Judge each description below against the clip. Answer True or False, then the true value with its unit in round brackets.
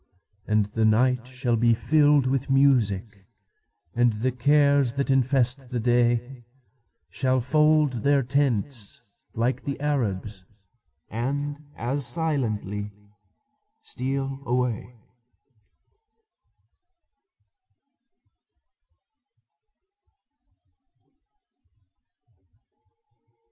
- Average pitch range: True (3.6 semitones)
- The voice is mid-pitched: False (125 Hz)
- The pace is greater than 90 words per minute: False (60 wpm)